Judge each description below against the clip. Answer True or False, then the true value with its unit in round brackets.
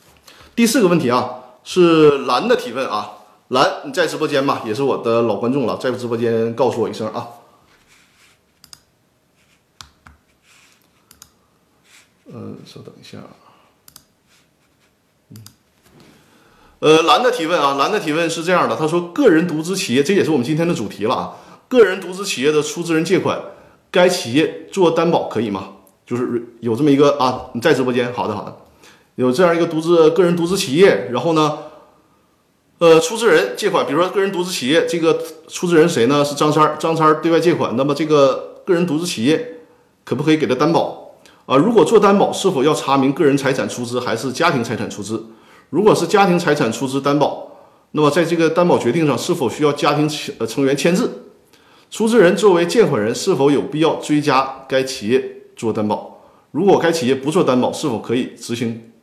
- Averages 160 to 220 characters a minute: False (280 characters per minute)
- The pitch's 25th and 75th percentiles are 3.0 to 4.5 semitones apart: False (5.0 semitones)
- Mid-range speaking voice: True (155 Hz)